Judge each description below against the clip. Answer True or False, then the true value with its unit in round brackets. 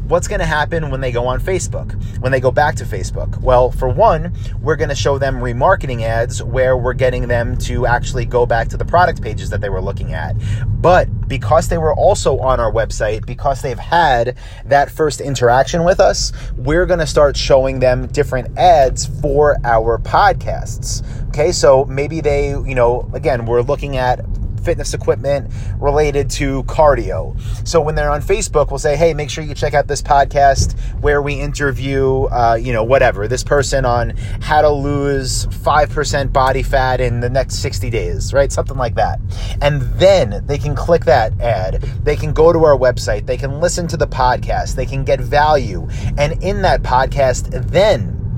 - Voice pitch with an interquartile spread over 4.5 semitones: False (3.9 semitones)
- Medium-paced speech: True (190 wpm)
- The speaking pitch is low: True (125 Hz)